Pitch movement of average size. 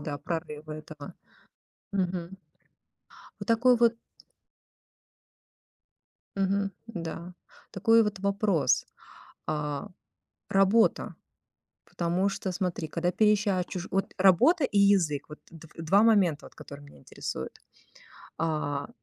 Yes: average, 4.3 semitones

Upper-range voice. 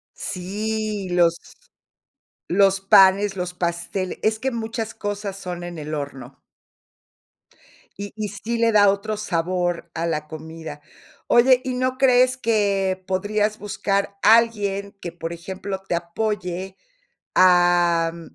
Yes: high, 195 Hz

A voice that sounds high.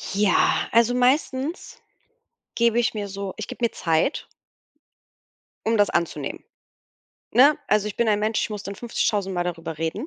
Yes: high, 210 Hz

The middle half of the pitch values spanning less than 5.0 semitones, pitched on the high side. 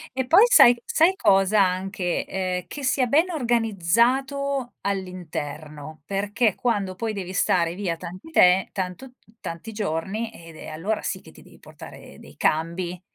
No: average, 5.3 semitones; high, 195 Hz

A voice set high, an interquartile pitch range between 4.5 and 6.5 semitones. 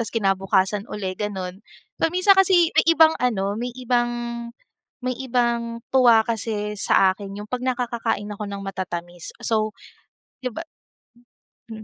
No: high, 220 Hz; average, 4.0 semitones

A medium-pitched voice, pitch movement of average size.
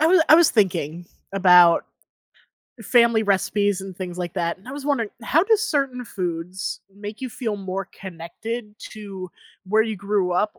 No: high, 205 Hz; average, 4.2 semitones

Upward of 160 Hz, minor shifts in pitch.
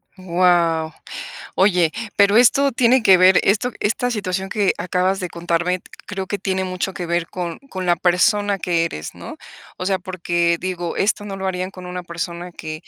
Yes: medium, 185 Hz; narrow, 2.2 semitones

